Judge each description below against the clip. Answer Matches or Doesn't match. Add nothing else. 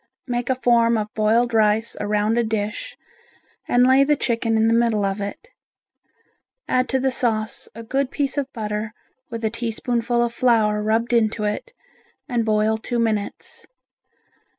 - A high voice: Matches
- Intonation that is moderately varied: Doesn't match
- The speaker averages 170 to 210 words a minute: Doesn't match